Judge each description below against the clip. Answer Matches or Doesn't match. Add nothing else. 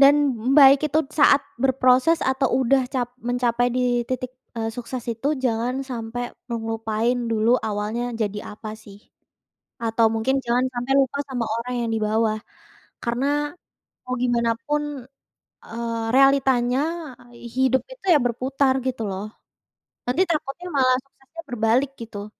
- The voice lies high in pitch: Matches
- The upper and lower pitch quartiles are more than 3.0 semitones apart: Doesn't match